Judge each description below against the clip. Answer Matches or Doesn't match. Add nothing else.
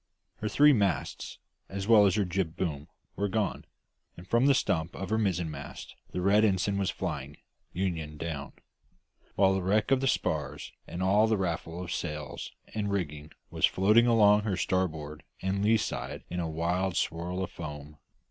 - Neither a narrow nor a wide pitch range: Matches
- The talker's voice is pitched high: Doesn't match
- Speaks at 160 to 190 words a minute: Matches